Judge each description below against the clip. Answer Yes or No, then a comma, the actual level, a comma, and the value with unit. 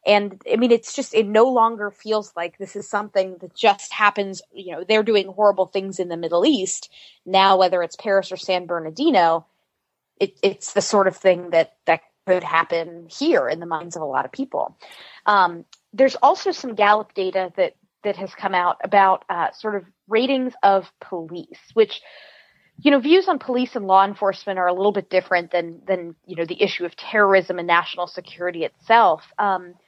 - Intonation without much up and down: No, average, 3.4 semitones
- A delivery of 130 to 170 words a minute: No, average, 195 wpm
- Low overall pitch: No, high, 195 Hz